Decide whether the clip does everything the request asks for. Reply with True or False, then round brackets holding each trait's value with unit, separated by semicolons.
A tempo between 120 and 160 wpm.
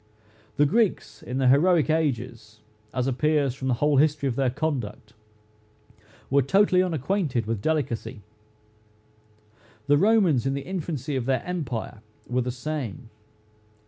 True (135 wpm)